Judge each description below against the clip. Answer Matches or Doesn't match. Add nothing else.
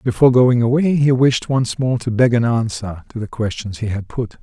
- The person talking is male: Matches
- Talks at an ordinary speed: Doesn't match